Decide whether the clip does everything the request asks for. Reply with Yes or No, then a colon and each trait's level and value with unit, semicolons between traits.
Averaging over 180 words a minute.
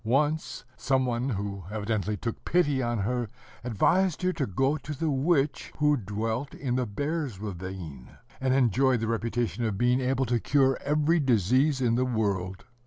No: average, 170 wpm